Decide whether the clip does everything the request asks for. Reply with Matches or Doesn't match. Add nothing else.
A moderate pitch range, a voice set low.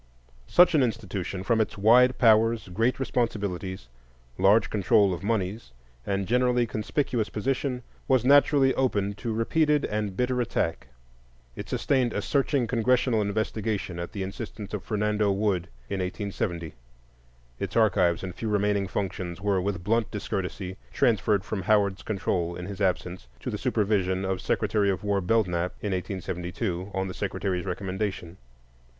Matches